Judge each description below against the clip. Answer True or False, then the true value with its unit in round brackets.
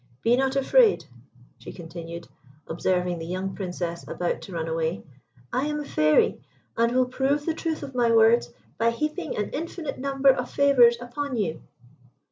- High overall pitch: True (235 Hz)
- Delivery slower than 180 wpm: True (165 wpm)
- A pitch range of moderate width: False (7.6 semitones)